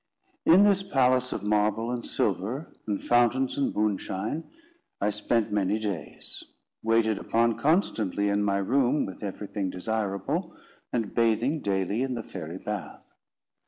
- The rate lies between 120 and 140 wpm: Yes, slow, 135 wpm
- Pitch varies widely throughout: No, average, 3.9 semitones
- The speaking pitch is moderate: No, low, 110 Hz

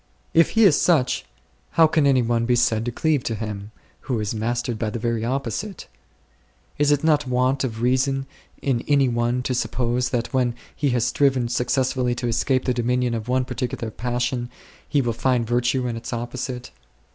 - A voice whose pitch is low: Yes, low, 125 Hz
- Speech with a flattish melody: Yes, narrow, 2.0 semitones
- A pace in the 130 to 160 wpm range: No, average, 185 wpm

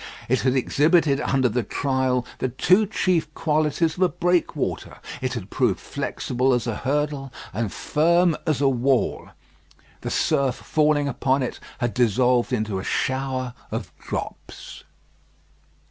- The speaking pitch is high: No, low, 135 Hz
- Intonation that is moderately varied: Yes, average, 3.4 semitones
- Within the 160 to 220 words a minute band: No, average, 140 wpm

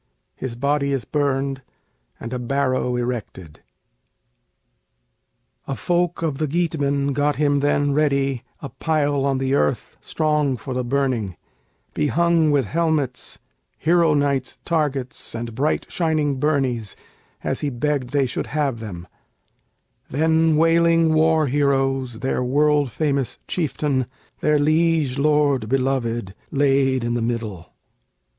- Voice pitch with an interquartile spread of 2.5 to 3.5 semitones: Yes, average, 2.9 semitones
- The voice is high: No, medium, 140 Hz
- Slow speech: Yes, slow, 125 wpm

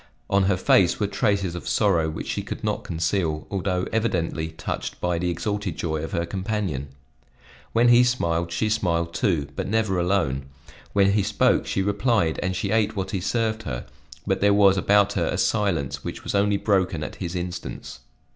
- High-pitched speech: No, very low, 95 Hz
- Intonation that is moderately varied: Yes, average, 3.4 semitones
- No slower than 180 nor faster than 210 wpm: Yes, average, 185 wpm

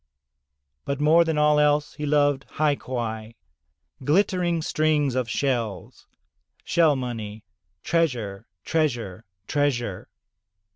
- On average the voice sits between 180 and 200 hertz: No, medium, 140 Hz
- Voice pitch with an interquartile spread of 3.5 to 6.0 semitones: Yes, average, 4.7 semitones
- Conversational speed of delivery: No, slow, 115 wpm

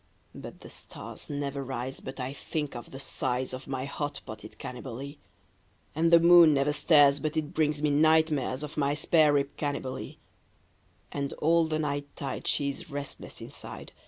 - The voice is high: No, medium, 145 Hz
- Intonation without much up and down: Yes, narrow, 2.1 semitones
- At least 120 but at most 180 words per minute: Yes, average, 175 wpm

